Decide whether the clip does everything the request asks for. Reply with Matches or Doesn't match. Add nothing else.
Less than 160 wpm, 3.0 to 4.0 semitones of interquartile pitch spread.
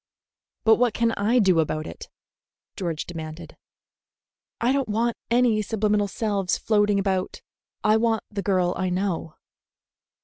Matches